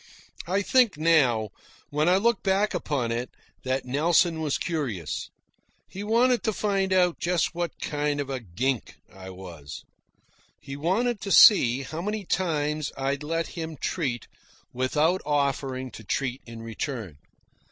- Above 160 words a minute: No, average, 145 wpm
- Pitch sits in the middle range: Yes, medium, 150 Hz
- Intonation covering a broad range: Yes, wide, 5.9 semitones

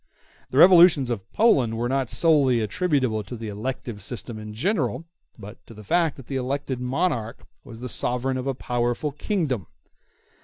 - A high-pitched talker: No, low, 125 Hz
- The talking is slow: No, average, 165 wpm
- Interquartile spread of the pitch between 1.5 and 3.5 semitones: No, average, 3.9 semitones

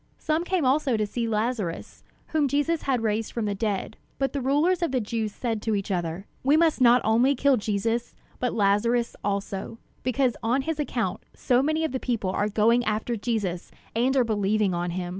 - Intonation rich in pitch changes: No, average, 4.3 semitones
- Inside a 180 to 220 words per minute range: Yes, average, 195 wpm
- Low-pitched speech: No, high, 230 Hz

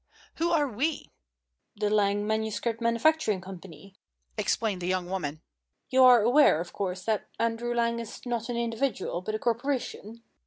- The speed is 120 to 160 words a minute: Yes, average, 155 wpm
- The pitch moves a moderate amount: Yes, average, 3.6 semitones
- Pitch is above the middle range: Yes, high, 225 Hz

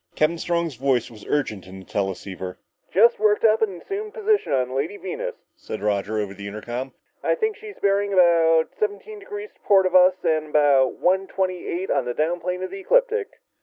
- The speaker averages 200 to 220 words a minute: Yes, fast, 205 wpm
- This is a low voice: No, medium, 175 Hz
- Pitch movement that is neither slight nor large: No, wide, 8.3 semitones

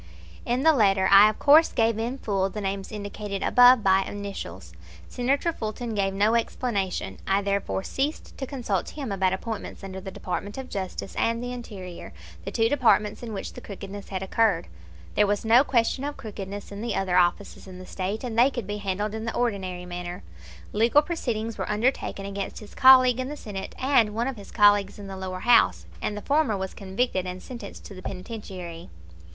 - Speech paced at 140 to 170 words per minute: No, average, 195 wpm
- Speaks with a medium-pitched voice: No, high, 205 Hz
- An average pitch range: Yes, average, 3.7 semitones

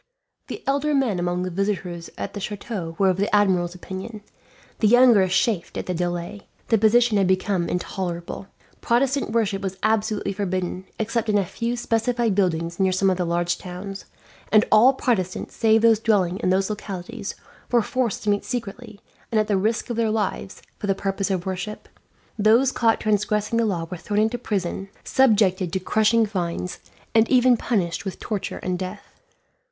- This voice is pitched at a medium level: No, high, 205 Hz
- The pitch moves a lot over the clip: No, average, 3.3 semitones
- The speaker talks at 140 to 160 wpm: No, average, 180 wpm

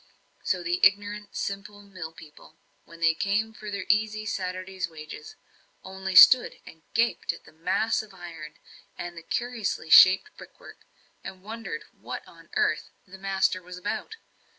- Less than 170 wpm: Yes, average, 150 wpm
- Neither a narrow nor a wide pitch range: Yes, average, 3.2 semitones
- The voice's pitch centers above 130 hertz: Yes, high, 190 Hz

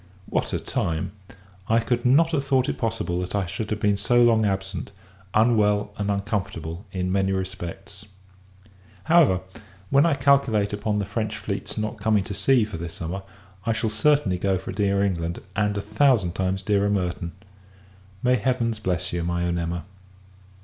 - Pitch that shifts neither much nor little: Yes, average, 3.4 semitones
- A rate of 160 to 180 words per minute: Yes, average, 170 wpm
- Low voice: Yes, low, 100 Hz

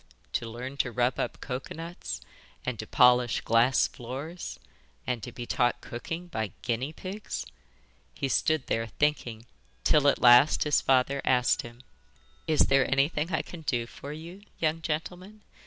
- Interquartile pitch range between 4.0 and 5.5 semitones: Yes, average, 4.5 semitones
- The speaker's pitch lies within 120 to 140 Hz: Yes, low, 135 Hz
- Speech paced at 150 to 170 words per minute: Yes, average, 155 wpm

